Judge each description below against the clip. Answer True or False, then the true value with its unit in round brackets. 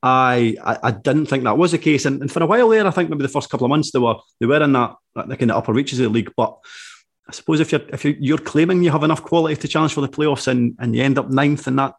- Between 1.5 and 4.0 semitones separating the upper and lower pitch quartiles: True (3.4 semitones)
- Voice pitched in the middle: True (145 Hz)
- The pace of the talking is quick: True (305 wpm)